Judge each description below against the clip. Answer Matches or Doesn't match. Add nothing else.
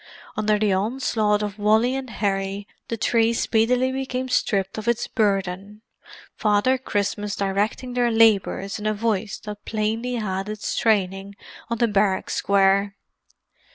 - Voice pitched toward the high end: Matches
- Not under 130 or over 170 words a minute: Matches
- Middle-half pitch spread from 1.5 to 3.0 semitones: Matches